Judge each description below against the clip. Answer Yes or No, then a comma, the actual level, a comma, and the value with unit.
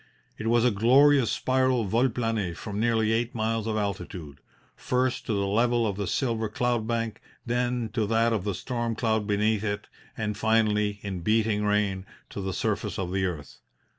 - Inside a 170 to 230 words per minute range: Yes, average, 180 wpm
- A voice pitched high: No, low, 110 Hz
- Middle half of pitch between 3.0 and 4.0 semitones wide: No, narrow, 2.5 semitones